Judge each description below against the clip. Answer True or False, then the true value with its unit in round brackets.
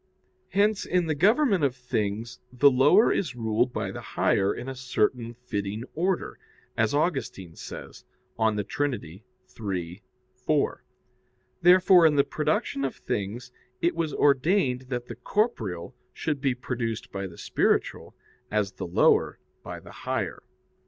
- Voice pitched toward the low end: True (125 Hz)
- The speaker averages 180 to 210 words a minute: False (140 wpm)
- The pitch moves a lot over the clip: True (5.7 semitones)